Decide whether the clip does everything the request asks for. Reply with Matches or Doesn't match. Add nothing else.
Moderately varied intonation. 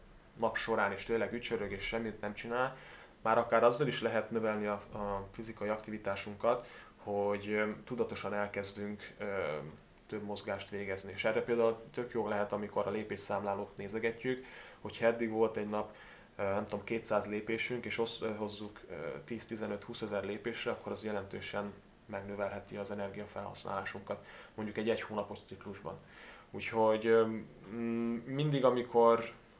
Doesn't match